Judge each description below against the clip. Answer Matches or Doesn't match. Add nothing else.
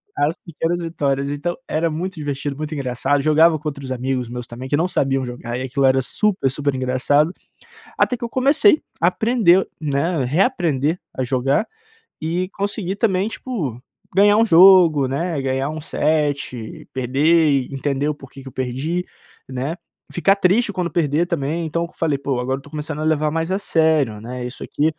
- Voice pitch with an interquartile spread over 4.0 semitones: Matches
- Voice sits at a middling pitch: Matches